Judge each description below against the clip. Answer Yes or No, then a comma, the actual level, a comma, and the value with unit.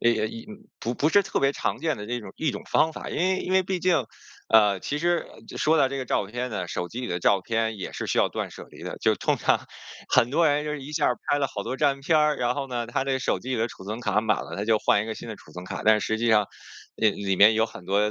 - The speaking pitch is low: Yes, low, 120 Hz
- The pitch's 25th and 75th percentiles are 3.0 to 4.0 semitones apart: No, average, 5.2 semitones